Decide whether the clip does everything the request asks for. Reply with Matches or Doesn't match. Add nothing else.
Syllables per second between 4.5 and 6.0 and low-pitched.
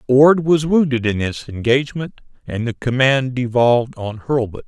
Matches